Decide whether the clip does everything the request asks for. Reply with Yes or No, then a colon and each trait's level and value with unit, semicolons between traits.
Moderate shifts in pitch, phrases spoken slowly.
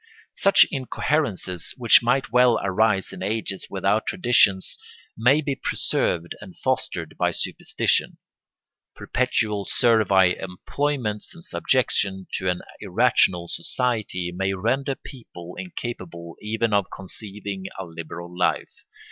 Yes: average, 4.9 semitones; slow, 115 wpm